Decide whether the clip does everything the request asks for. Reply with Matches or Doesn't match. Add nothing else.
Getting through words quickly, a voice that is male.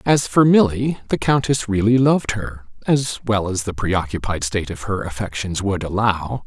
Doesn't match